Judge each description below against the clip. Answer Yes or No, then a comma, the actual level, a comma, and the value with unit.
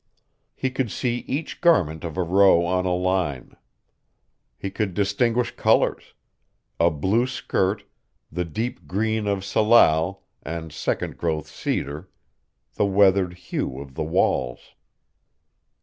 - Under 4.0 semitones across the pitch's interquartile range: No, average, 4.6 semitones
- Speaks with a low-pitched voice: Yes, very low, 95 Hz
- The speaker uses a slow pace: Yes, slow, 125 wpm